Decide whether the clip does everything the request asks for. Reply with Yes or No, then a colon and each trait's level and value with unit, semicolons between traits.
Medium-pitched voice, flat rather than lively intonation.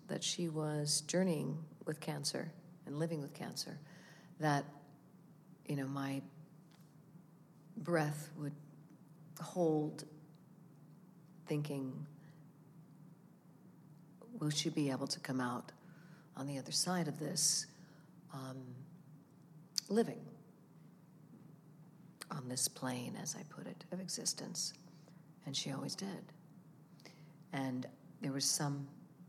Yes: medium, 160 Hz; narrow, 2.3 semitones